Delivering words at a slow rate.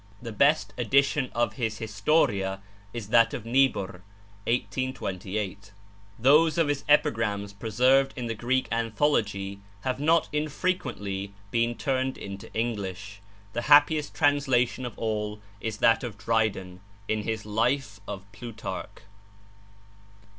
Yes: slow, 120 wpm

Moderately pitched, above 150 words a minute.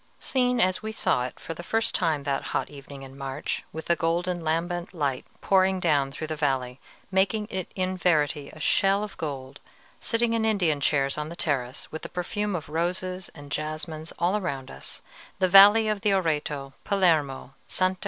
Yes: medium, 165 Hz; average, 185 wpm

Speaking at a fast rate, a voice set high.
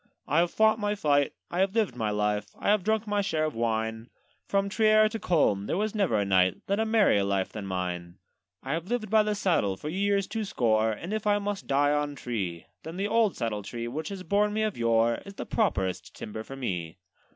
No: fast, 230 wpm; medium, 155 Hz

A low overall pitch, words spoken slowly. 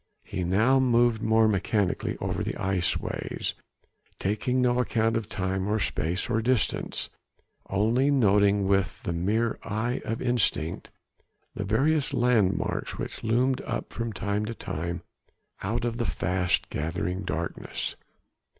Yes: low, 110 Hz; slow, 130 wpm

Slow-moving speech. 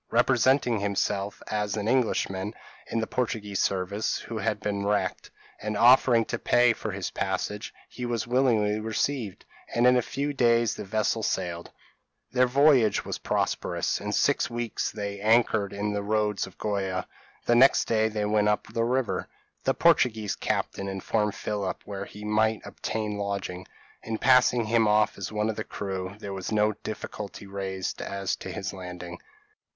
No: average, 165 wpm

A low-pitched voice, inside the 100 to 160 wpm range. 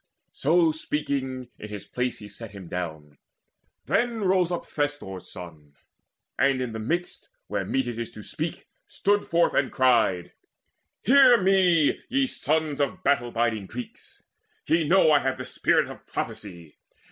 Yes: low, 130 Hz; average, 155 wpm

